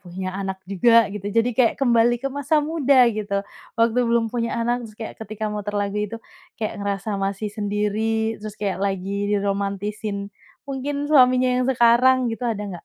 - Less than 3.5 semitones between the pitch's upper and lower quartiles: Yes, average, 3.1 semitones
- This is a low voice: No, high, 220 Hz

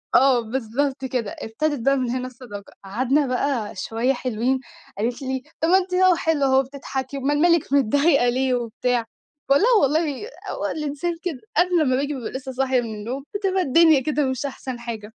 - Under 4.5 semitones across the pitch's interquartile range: Yes, average, 3.1 semitones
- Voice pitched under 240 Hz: No, very high, 265 Hz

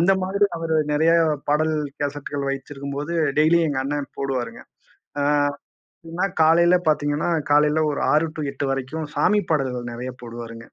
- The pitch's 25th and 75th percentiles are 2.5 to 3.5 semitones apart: Yes, average, 3.0 semitones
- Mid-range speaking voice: Yes, medium, 145 Hz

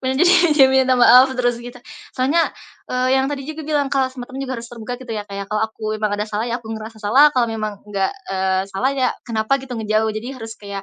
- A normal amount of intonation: Yes, average, 3.5 semitones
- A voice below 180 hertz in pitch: No, high, 240 Hz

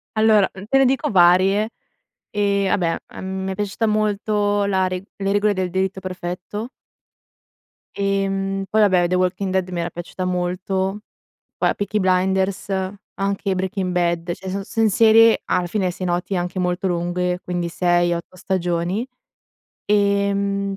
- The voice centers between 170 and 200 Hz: Yes, high, 190 Hz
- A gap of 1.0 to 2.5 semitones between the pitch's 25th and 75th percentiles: Yes, narrow, 1.9 semitones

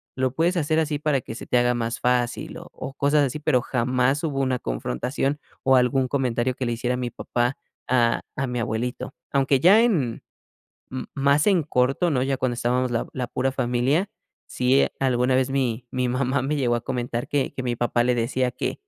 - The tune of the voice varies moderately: No, narrow, 2.2 semitones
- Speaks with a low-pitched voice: Yes, low, 130 Hz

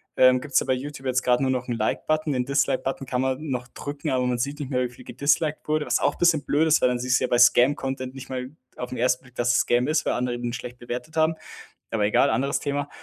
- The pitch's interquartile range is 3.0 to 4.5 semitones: No, narrow, 2.5 semitones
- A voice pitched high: No, low, 130 Hz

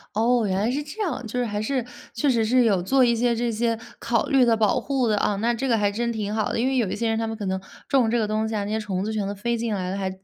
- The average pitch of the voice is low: No, high, 225 Hz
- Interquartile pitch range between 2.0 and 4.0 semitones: Yes, narrow, 2.5 semitones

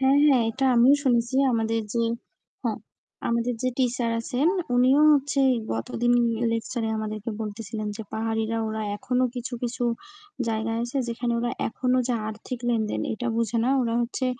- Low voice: No, high, 235 Hz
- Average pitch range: No, narrow, 2.0 semitones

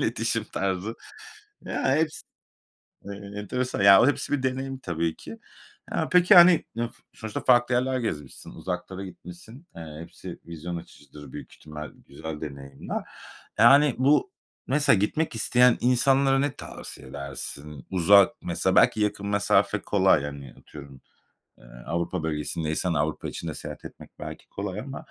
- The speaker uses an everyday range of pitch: No, wide, 8.6 semitones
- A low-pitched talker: Yes, low, 100 Hz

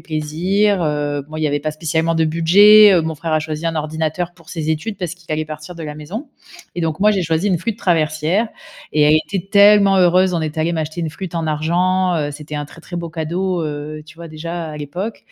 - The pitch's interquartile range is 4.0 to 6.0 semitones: No, average, 2.9 semitones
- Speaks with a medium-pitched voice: Yes, medium, 165 Hz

